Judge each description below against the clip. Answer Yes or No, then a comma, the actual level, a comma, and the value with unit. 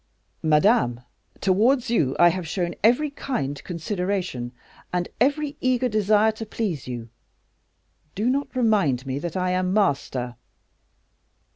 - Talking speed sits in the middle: No, slow, 125 wpm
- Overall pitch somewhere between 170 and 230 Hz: Yes, medium, 185 Hz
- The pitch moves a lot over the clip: Yes, wide, 7.2 semitones